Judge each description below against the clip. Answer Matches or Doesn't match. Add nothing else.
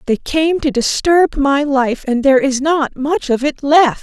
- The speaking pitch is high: Matches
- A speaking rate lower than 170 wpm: Doesn't match